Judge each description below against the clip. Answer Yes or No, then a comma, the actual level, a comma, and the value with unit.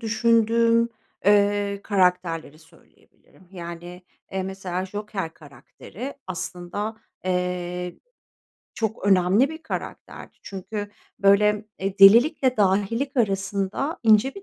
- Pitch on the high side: Yes, high, 200 Hz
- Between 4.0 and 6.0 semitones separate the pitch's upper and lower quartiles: No, average, 3.6 semitones